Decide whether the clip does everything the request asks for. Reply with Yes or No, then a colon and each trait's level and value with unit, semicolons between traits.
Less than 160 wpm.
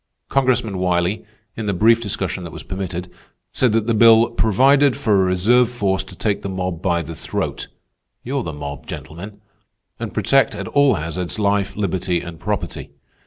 No: average, 165 wpm